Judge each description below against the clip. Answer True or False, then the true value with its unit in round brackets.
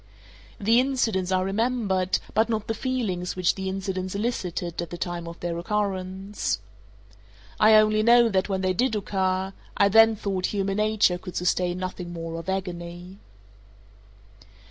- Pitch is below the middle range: False (190 Hz)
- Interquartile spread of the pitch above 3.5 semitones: False (2.9 semitones)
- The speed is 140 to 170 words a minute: True (150 wpm)